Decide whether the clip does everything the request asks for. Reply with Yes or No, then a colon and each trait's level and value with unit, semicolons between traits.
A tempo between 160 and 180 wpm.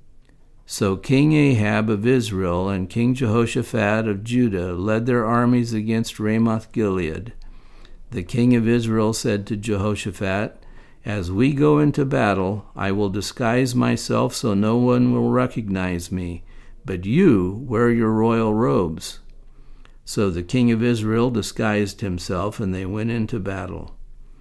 No: average, 140 wpm